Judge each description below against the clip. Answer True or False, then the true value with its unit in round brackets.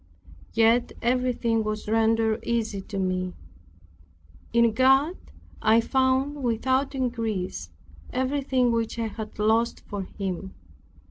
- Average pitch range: True (3.1 semitones)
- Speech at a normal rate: False (110 wpm)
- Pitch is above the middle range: True (230 Hz)